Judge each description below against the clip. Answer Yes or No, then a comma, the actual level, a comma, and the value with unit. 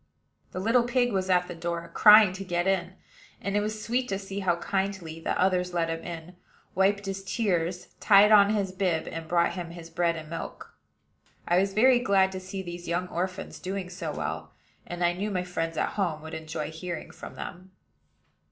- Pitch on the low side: No, medium, 185 Hz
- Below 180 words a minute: No, average, 200 wpm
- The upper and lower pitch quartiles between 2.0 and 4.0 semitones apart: Yes, narrow, 2.5 semitones